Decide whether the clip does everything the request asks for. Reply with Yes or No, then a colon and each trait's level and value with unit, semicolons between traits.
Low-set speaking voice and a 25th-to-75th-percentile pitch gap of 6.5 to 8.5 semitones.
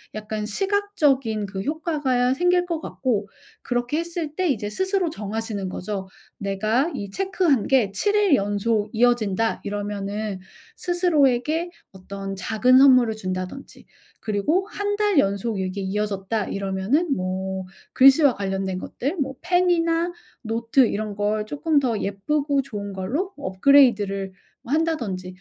No: high, 230 Hz; wide, 7.3 semitones